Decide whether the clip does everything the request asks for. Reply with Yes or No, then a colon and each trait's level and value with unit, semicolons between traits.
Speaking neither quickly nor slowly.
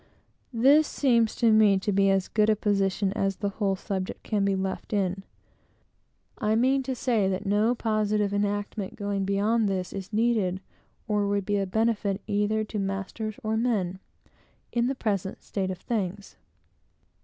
Yes: average, 165 wpm